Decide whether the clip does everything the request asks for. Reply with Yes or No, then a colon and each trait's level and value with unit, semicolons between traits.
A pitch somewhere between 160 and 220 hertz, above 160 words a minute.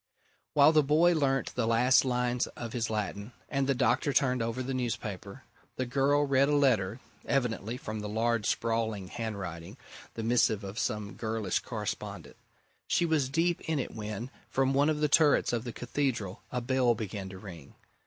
No: low, 120 Hz; average, 175 wpm